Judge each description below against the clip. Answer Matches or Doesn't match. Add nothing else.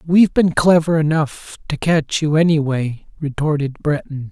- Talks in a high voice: Doesn't match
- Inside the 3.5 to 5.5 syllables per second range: Matches